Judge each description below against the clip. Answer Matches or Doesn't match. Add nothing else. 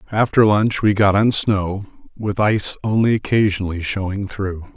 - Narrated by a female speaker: Doesn't match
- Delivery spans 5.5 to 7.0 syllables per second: Doesn't match